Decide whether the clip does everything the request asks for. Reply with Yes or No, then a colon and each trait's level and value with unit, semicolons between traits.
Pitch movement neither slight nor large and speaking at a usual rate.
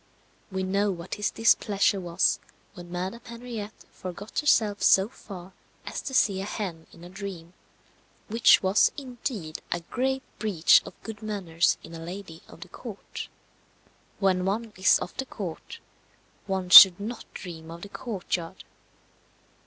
Yes: average, 3.6 semitones; average, 150 wpm